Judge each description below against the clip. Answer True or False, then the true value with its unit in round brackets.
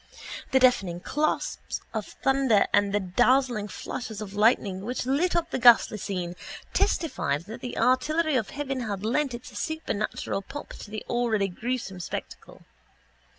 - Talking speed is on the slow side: False (150 wpm)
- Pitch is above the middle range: True (235 Hz)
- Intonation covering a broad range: False (4.7 semitones)